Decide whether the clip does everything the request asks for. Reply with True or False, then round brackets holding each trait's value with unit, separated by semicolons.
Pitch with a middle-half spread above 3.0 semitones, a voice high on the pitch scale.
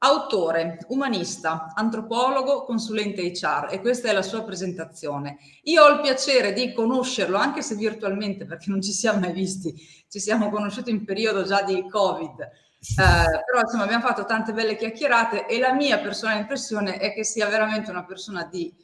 True (3.5 semitones; 210 Hz)